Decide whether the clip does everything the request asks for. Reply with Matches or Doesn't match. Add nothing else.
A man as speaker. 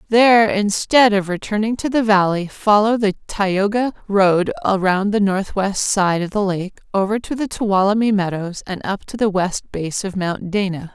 Doesn't match